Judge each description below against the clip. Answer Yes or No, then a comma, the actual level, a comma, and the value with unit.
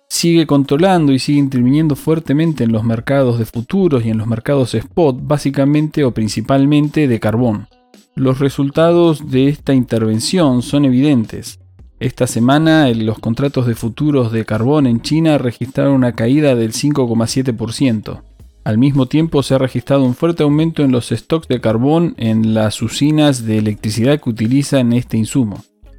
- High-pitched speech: No, low, 130 Hz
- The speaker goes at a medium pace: Yes, average, 150 wpm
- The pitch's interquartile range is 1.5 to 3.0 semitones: No, average, 4.3 semitones